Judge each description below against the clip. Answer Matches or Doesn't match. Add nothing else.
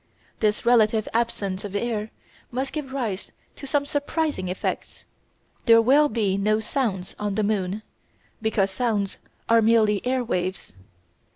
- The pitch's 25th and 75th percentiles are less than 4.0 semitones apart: Matches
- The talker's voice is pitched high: Matches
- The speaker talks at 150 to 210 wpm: Doesn't match